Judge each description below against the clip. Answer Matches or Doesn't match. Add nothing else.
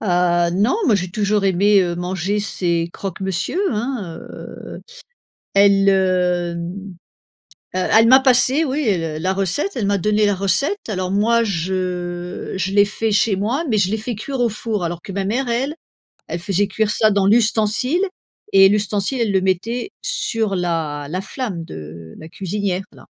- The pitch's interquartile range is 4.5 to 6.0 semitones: Doesn't match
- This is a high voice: Matches